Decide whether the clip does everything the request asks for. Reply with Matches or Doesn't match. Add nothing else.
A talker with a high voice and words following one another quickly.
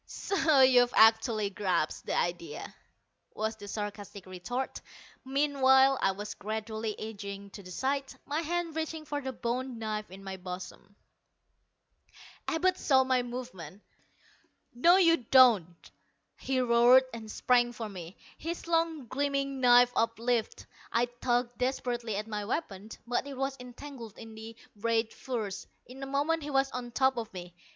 Doesn't match